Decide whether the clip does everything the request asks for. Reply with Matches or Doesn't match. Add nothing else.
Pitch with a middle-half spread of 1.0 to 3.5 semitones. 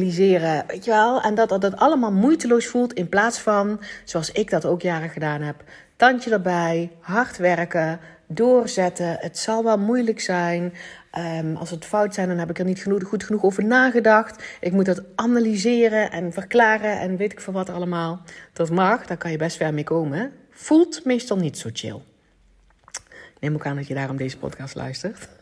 Doesn't match